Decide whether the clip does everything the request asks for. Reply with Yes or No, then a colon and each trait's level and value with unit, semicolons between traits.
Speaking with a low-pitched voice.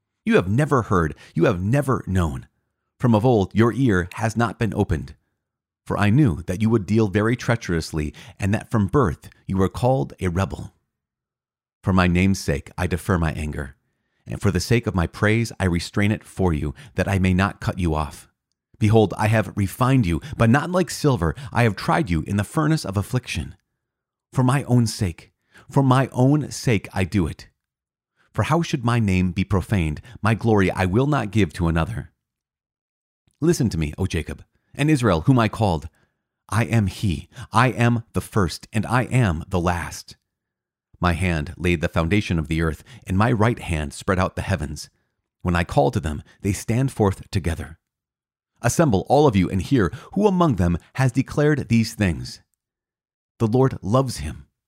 Yes: low, 100 Hz